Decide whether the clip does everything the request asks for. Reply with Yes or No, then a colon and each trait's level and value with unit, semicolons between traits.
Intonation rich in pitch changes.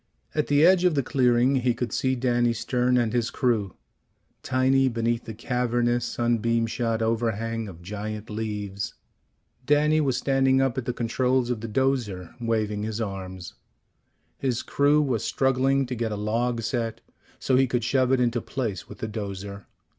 No: average, 2.9 semitones